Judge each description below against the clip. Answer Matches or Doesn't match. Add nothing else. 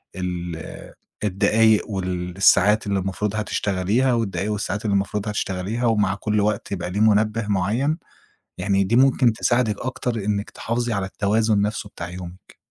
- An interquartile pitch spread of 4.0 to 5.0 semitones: Doesn't match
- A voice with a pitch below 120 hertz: Matches